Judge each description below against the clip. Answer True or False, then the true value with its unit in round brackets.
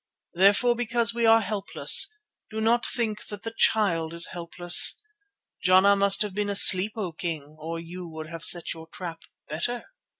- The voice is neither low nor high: False (195 Hz)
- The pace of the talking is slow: False (165 wpm)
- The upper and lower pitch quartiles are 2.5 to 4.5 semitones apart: False (4.9 semitones)